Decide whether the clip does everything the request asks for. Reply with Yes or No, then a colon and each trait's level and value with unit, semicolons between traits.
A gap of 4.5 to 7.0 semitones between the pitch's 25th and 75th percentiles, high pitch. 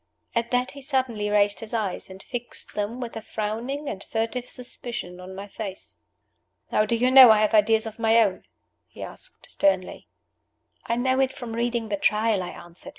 No: average, 2.9 semitones; high, 225 Hz